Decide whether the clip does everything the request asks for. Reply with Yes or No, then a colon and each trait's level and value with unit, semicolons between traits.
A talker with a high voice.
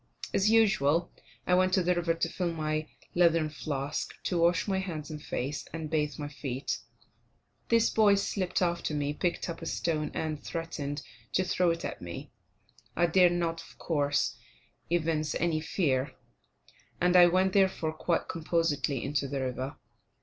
No: medium, 165 Hz